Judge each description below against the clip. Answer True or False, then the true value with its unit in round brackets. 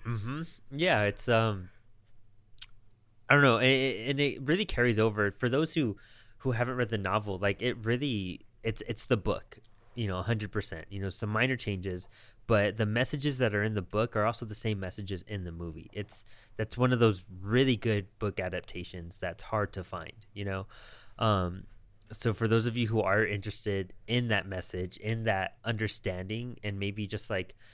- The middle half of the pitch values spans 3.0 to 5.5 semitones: False (2.6 semitones)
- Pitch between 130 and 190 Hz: False (110 Hz)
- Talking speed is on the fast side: False (190 wpm)